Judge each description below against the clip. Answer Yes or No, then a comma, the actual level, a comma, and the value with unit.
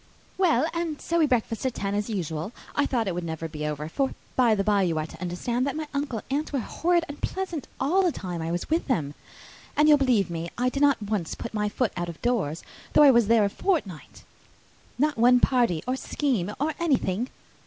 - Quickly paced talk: Yes, fast, 225 wpm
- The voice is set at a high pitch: Yes, high, 235 Hz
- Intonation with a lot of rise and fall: Yes, wide, 7.9 semitones